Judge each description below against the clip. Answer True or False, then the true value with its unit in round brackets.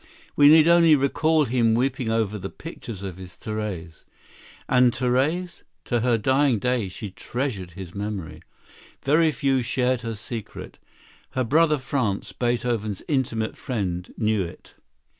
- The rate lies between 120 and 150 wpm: True (140 wpm)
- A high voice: False (120 Hz)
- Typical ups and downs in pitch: True (4.5 semitones)